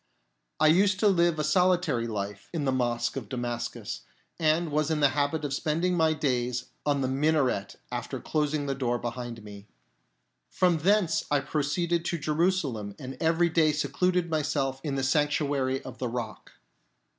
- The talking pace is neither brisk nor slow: Yes, average, 160 wpm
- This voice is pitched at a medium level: Yes, medium, 145 Hz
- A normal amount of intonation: Yes, average, 4.2 semitones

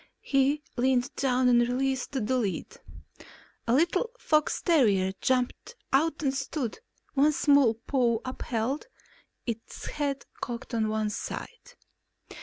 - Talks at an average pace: No, slow, 120 wpm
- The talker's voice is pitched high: Yes, very high, 260 Hz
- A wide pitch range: No, average, 3.3 semitones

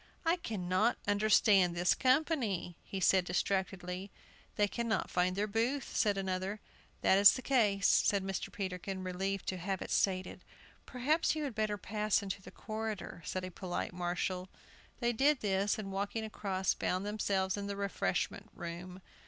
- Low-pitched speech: No, high, 200 Hz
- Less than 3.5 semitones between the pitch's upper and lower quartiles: Yes, narrow, 2.6 semitones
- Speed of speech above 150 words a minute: Yes, average, 160 wpm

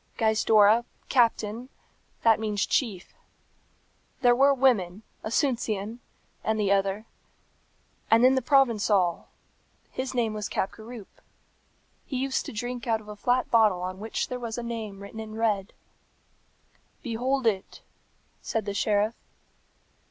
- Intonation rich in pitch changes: No, average, 2.9 semitones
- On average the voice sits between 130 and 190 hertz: No, high, 225 Hz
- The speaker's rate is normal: No, slow, 130 wpm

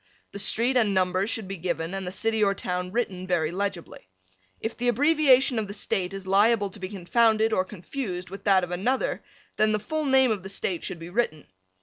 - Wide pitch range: No, average, 3.7 semitones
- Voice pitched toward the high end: Yes, high, 200 Hz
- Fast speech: Yes, fast, 215 wpm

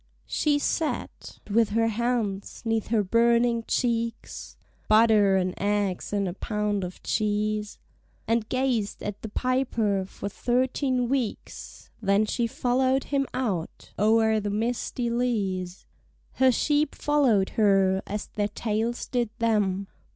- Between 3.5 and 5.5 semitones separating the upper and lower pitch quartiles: No, average, 3.0 semitones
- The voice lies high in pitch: Yes, high, 220 Hz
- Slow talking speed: Yes, slow, 130 wpm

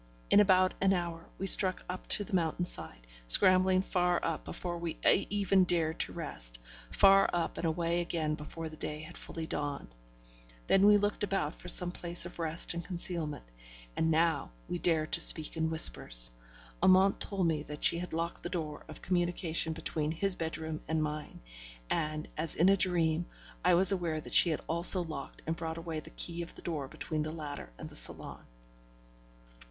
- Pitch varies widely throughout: No, narrow, 2.4 semitones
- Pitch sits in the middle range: Yes, medium, 170 Hz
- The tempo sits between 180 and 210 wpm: Yes, average, 185 wpm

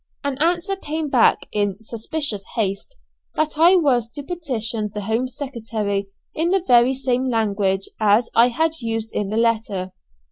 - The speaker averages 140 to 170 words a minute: Yes, average, 155 wpm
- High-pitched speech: Yes, high, 235 Hz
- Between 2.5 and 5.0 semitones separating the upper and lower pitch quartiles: No, wide, 5.5 semitones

